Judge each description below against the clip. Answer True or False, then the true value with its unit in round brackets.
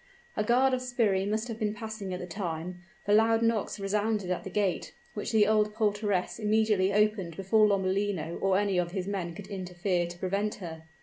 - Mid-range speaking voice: False (205 Hz)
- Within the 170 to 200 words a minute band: True (195 wpm)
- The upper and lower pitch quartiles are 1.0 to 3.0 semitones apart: True (2.6 semitones)